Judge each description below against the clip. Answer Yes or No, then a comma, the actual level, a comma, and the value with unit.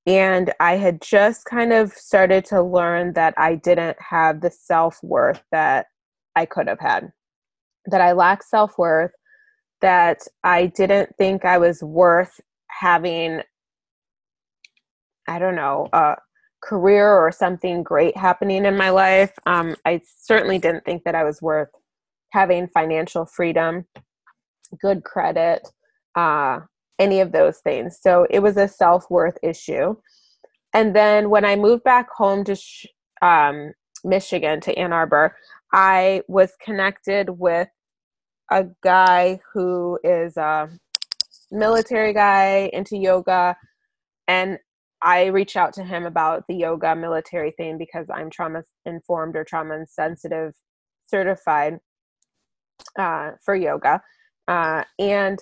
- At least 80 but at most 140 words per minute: Yes, slow, 135 wpm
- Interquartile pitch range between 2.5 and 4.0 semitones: Yes, average, 2.8 semitones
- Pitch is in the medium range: Yes, medium, 180 Hz